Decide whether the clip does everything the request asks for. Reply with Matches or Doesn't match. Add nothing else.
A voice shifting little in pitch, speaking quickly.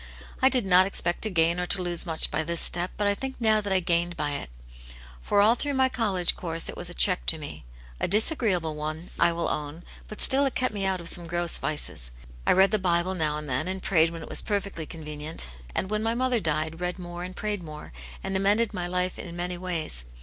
Doesn't match